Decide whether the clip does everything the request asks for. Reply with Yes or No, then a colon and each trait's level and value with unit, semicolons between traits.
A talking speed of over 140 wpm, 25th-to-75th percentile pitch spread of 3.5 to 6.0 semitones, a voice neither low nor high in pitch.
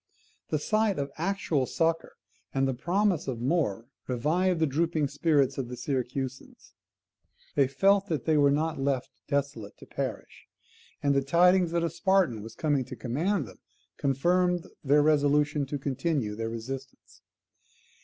Yes: average, 150 wpm; average, 4.2 semitones; medium, 145 Hz